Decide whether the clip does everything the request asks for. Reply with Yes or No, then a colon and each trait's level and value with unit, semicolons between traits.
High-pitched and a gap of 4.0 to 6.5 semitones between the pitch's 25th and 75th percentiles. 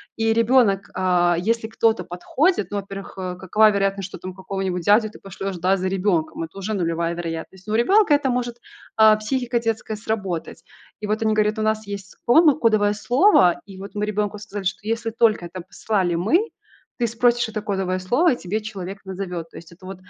No: high, 205 Hz; average, 3.2 semitones